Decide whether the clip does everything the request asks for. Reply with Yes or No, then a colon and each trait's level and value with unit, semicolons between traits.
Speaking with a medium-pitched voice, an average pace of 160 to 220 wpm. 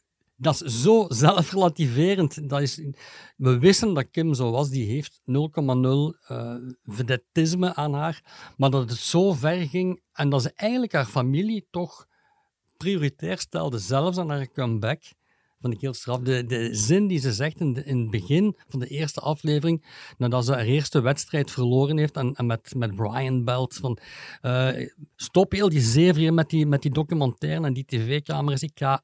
Yes: medium, 145 Hz; average, 170 wpm